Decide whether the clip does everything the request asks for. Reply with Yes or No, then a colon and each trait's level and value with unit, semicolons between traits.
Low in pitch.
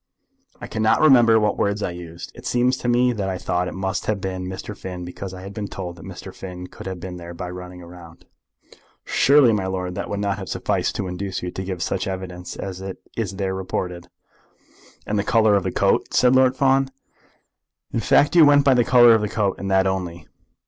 Yes: very low, 95 Hz